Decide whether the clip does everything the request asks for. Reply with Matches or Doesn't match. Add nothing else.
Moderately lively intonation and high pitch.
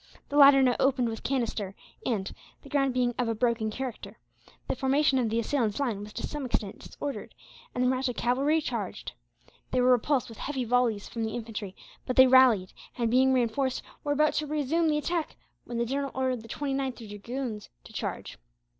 Matches